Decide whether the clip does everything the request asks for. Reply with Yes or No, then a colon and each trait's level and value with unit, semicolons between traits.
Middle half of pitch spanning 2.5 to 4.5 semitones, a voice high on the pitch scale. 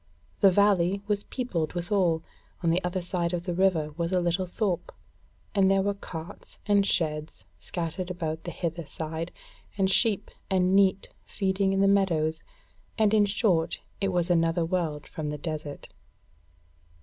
No: average, 2.9 semitones; medium, 180 Hz